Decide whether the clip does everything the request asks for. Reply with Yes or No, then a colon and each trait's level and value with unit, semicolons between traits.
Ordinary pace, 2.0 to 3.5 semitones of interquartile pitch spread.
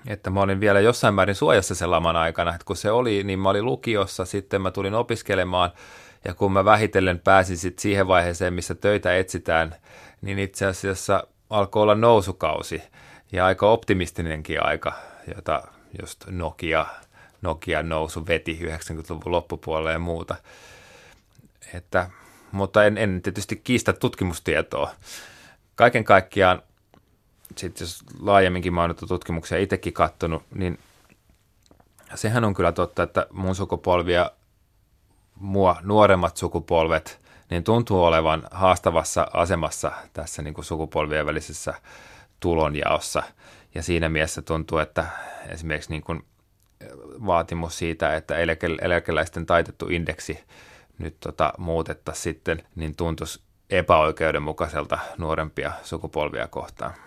Yes: average, 120 wpm; average, 3.2 semitones